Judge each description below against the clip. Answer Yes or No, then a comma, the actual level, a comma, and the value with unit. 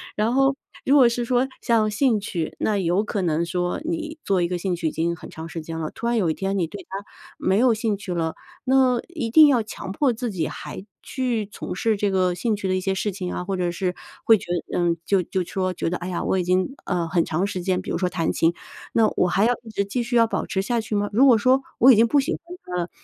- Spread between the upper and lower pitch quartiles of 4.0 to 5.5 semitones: Yes, average, 4.7 semitones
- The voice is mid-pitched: No, high, 200 Hz